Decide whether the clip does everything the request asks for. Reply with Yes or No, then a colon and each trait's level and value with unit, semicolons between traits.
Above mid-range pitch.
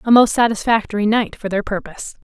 Yes: high, 215 Hz